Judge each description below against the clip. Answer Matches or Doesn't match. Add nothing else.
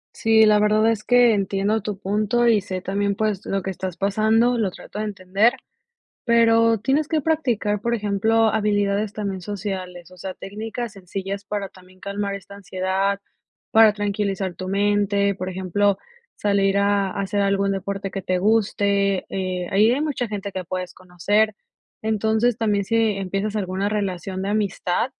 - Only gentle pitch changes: Matches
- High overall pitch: Matches